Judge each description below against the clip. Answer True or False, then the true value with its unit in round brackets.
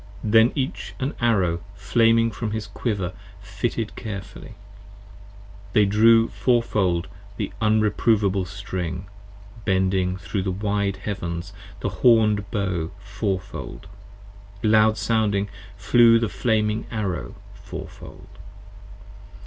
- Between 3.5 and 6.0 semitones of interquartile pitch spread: False (2.9 semitones)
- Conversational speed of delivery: False (105 wpm)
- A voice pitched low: True (105 Hz)